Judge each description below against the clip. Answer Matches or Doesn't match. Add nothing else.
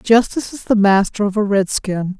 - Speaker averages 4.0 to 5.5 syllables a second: Matches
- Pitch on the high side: Matches